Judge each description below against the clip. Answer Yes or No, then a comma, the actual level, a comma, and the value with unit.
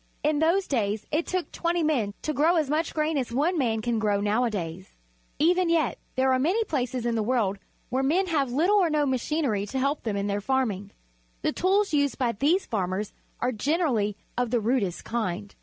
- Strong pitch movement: Yes, wide, 6.5 semitones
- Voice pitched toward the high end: Yes, very high, 260 Hz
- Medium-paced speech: No, fast, 210 wpm